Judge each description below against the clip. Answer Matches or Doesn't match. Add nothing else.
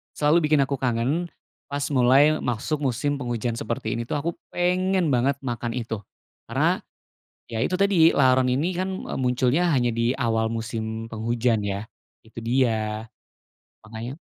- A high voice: Doesn't match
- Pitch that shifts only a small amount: Doesn't match